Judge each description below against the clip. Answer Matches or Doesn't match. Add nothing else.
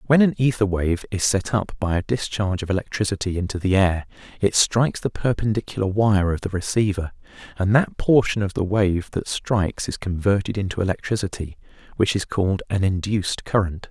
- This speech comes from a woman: Doesn't match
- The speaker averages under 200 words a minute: Matches